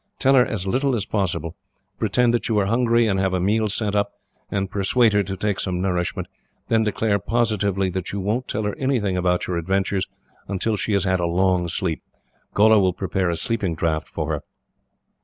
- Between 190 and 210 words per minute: Yes, average, 200 wpm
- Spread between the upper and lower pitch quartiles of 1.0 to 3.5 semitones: Yes, average, 3.0 semitones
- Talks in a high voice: No, low, 100 Hz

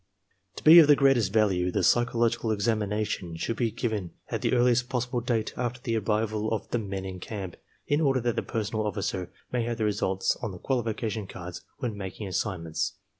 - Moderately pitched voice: No, low, 110 Hz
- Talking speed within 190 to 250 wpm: Yes, average, 195 wpm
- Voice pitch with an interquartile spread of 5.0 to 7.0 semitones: No, average, 3.6 semitones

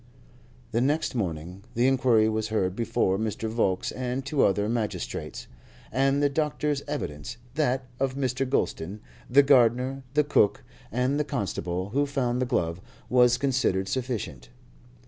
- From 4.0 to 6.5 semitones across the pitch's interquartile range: Yes, average, 4.7 semitones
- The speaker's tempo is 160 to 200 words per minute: No, average, 145 wpm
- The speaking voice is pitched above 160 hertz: No, low, 125 Hz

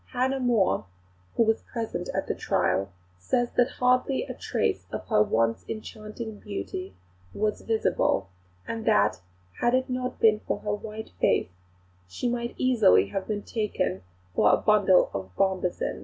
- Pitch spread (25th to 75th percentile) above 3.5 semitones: Yes, average, 4.4 semitones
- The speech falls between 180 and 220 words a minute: No, average, 155 wpm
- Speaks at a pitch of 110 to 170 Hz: No, high, 215 Hz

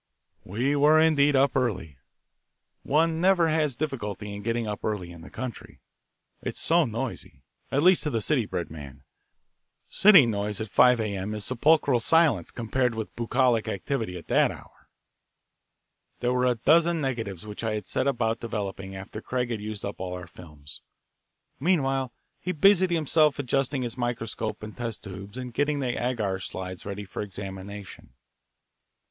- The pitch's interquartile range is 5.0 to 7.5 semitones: Yes, wide, 5.5 semitones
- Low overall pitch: Yes, low, 115 Hz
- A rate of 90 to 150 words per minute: No, average, 160 wpm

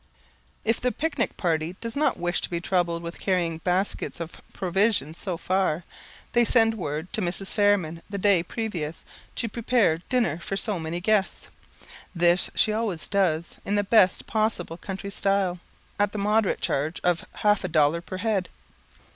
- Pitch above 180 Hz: Yes, high, 190 Hz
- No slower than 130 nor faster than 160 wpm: No, average, 170 wpm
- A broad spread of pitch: No, average, 3.8 semitones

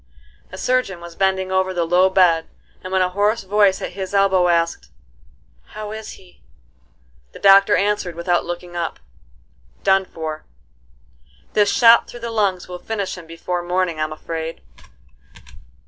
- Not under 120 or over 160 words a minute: Yes, average, 150 wpm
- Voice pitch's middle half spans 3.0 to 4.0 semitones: No, narrow, 2.4 semitones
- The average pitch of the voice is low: No, medium, 185 Hz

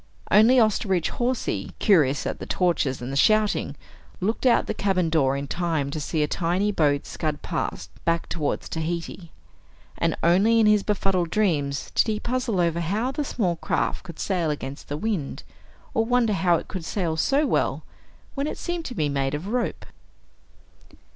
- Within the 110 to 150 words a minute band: No, average, 175 wpm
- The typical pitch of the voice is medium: Yes, medium, 180 Hz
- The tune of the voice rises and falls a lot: Yes, wide, 5.7 semitones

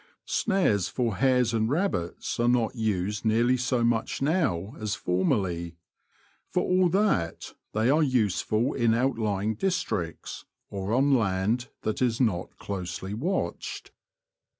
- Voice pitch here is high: No, low, 115 Hz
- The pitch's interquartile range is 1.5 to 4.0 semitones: No, average, 4.7 semitones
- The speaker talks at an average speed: No, slow, 125 wpm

